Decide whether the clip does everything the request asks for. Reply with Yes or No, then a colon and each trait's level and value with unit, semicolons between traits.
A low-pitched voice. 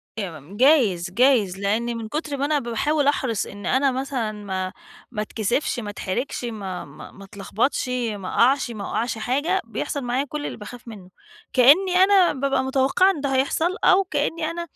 No: very high, 250 Hz